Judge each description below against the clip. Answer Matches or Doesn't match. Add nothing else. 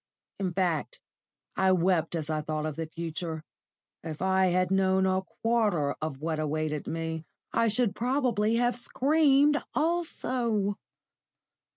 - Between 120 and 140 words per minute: Matches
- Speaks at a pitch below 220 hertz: Matches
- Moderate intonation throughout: Doesn't match